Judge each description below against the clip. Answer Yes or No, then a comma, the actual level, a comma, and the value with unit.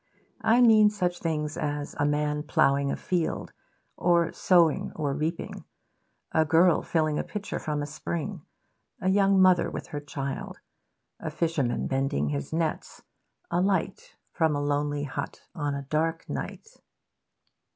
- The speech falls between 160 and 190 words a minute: No, average, 145 wpm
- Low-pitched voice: No, medium, 155 Hz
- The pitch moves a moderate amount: Yes, average, 3.4 semitones